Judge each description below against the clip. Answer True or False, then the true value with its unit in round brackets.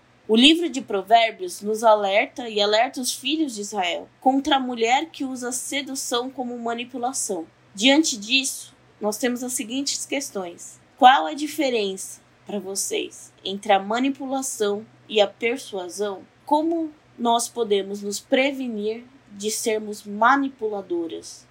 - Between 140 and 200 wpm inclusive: False (130 wpm)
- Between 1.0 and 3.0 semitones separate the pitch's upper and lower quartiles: False (4.5 semitones)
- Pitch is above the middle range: True (235 Hz)